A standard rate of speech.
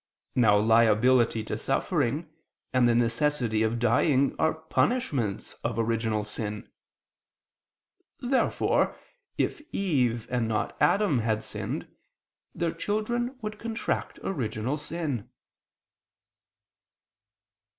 No: slow, 95 wpm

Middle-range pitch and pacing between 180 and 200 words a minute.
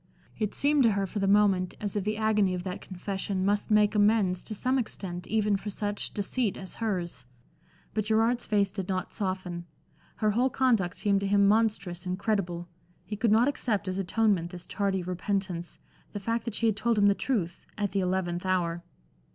No: high, 200 Hz; average, 190 wpm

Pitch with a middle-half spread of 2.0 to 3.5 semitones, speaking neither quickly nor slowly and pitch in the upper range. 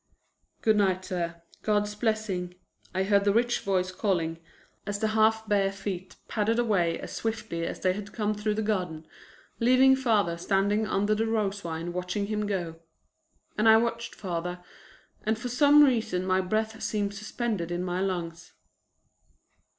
Yes: average, 3.2 semitones; average, 160 wpm; high, 205 Hz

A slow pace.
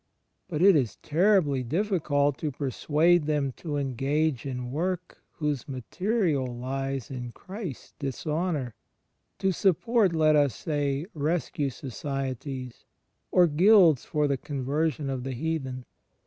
Yes: slow, 125 wpm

